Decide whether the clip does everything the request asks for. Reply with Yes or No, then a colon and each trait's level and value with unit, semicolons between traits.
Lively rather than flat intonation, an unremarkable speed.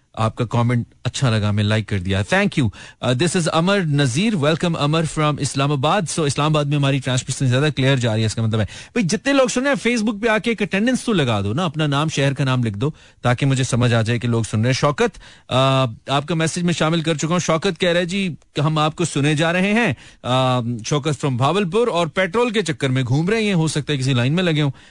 No: wide, 5.7 semitones; fast, 220 wpm